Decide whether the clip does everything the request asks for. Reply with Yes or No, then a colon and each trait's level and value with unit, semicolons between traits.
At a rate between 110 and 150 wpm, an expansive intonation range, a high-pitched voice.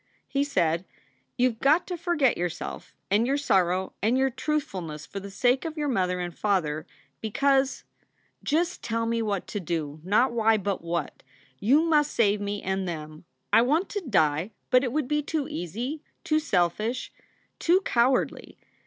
No: average, 170 wpm; wide, 7.5 semitones; high, 225 Hz